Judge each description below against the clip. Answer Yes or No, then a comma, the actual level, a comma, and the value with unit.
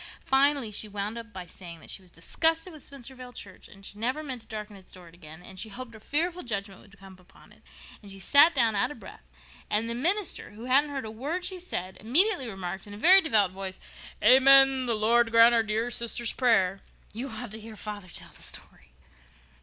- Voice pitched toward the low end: No, high, 225 Hz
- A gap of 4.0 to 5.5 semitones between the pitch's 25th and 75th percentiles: Yes, average, 5.2 semitones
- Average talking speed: No, fast, 220 wpm